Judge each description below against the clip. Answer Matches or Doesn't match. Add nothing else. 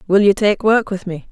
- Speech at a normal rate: Doesn't match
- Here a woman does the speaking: Matches